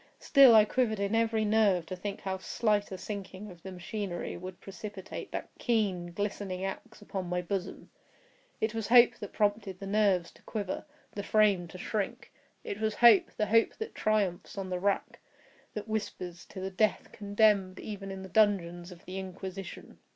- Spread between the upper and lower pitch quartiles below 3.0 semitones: Yes, narrow, 2.5 semitones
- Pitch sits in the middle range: No, high, 200 Hz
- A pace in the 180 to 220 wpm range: No, average, 170 wpm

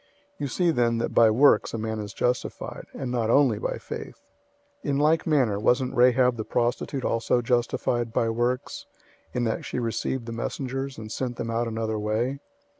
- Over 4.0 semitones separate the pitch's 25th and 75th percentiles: No, narrow, 2.6 semitones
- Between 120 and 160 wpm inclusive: No, average, 190 wpm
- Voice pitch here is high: No, low, 120 Hz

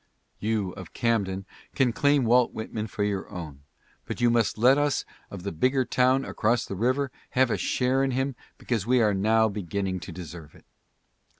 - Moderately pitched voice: No, low, 110 Hz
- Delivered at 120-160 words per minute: No, average, 185 wpm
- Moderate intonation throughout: Yes, average, 4.6 semitones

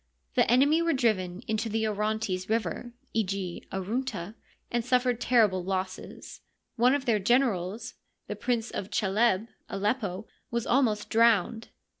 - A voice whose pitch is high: Yes, high, 220 Hz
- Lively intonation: No, average, 3.8 semitones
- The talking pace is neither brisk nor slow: No, slow, 130 wpm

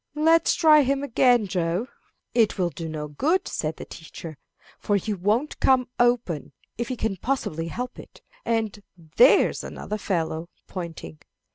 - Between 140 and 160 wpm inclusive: Yes, average, 150 wpm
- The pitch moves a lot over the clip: Yes, wide, 7.1 semitones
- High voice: Yes, high, 210 Hz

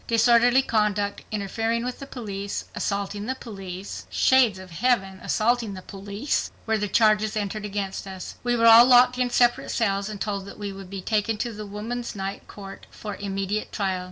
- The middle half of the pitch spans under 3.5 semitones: Yes, average, 2.9 semitones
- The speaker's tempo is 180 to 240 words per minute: Yes, average, 185 wpm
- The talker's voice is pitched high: Yes, high, 210 Hz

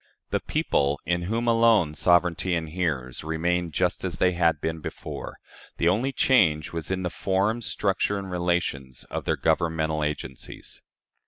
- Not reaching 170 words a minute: Yes, average, 150 wpm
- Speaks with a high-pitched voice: No, very low, 85 Hz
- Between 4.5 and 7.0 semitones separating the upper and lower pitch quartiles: No, average, 3.2 semitones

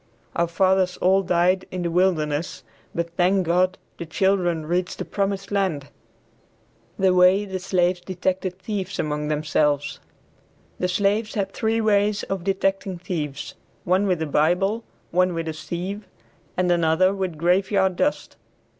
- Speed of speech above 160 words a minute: No, average, 145 wpm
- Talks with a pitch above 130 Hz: Yes, medium, 185 Hz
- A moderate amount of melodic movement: No, narrow, 2.3 semitones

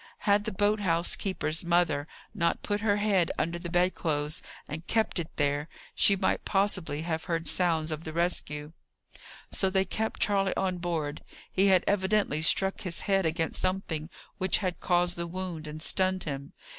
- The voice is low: No, medium, 175 Hz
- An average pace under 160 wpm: No, average, 175 wpm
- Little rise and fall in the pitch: No, average, 3.2 semitones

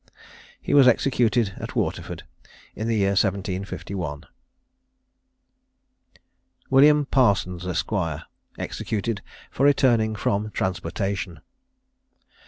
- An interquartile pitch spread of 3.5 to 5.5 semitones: Yes, average, 4.2 semitones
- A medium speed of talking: No, slow, 80 wpm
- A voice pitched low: Yes, low, 100 Hz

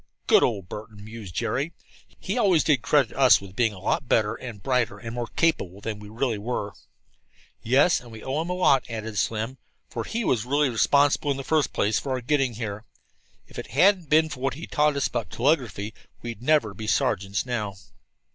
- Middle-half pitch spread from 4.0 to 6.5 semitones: Yes, average, 4.9 semitones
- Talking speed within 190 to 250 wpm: Yes, fast, 205 wpm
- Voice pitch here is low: Yes, low, 120 Hz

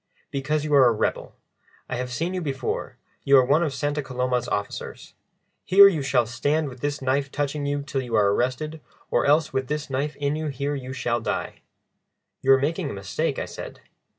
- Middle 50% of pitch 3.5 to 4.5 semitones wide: No, average, 2.8 semitones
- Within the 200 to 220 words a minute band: Yes, fast, 205 wpm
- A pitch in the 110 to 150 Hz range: Yes, medium, 140 Hz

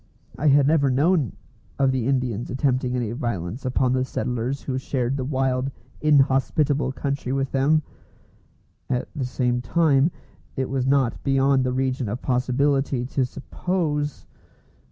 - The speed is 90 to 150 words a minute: Yes, average, 140 wpm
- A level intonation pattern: Yes, narrow, 1.8 semitones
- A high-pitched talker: No, low, 135 Hz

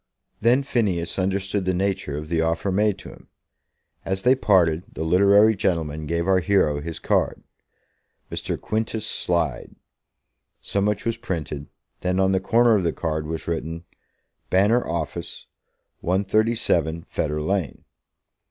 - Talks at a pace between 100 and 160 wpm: Yes, average, 140 wpm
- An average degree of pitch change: Yes, average, 3.8 semitones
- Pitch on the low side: Yes, very low, 95 Hz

